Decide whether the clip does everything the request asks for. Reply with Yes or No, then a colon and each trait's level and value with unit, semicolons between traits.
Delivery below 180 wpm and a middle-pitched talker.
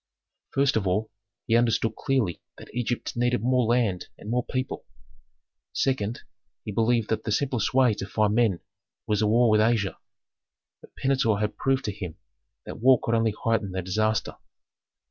No: average, 165 wpm; low, 115 Hz